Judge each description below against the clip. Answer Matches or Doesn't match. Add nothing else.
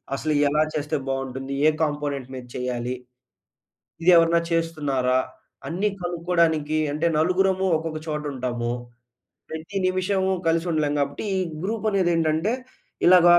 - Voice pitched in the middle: Matches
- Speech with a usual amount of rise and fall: Matches